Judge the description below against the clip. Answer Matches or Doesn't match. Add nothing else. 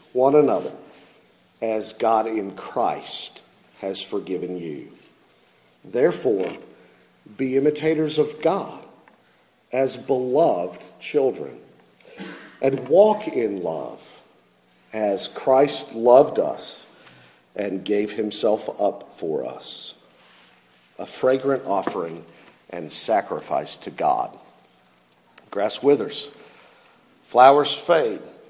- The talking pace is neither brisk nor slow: Doesn't match